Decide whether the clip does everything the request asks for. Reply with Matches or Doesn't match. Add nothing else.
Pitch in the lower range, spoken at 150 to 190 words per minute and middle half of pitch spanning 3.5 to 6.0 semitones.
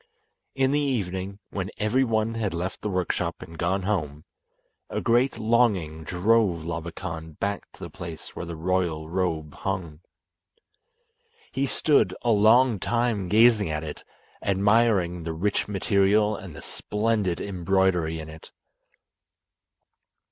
Doesn't match